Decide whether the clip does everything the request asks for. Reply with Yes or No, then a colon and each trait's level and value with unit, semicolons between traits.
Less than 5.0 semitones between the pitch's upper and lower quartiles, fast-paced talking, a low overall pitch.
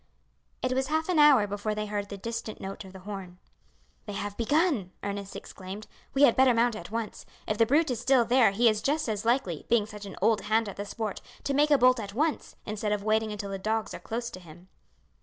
No: average, 3.7 semitones; fast, 235 wpm; high, 220 Hz